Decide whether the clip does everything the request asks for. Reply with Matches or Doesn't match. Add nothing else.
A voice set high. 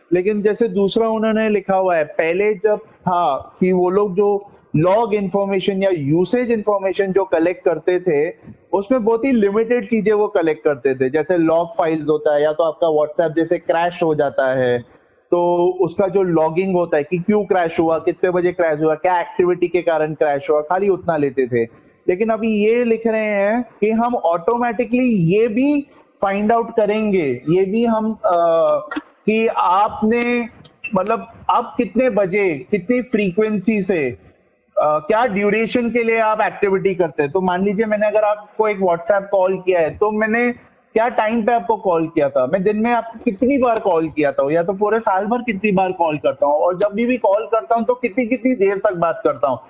Matches